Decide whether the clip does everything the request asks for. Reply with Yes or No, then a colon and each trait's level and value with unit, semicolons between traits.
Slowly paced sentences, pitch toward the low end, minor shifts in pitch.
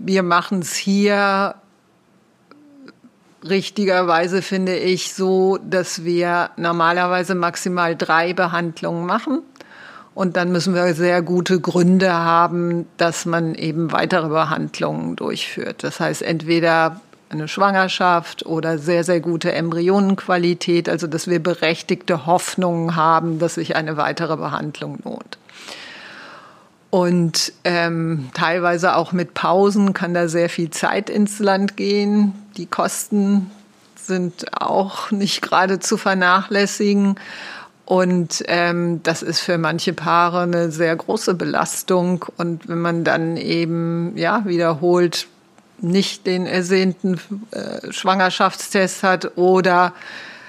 No: slow, 115 wpm; medium, 180 Hz; narrow, 2.2 semitones